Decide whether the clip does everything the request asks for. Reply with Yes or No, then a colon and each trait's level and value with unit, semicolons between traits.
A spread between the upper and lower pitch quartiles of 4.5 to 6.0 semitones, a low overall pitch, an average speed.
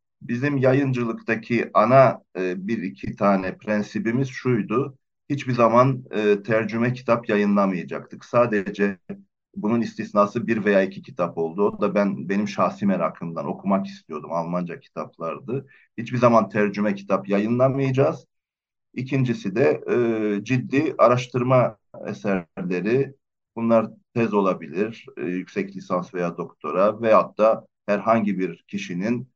No: average, 3.7 semitones; low, 110 Hz; average, 115 wpm